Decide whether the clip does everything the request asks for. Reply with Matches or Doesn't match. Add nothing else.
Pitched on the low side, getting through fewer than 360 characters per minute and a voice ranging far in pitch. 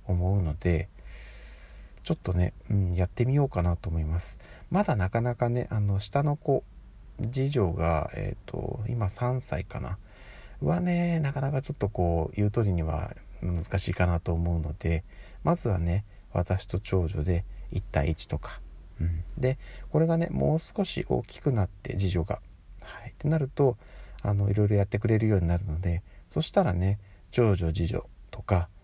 Matches